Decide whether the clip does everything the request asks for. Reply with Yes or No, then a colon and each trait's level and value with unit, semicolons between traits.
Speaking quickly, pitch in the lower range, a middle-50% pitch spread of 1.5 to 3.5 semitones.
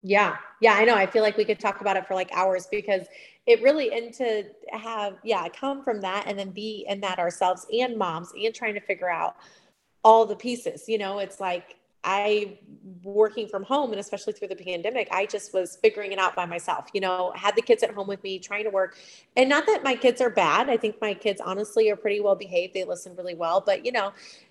No: fast, 240 wpm; high, 205 Hz; average, 2.7 semitones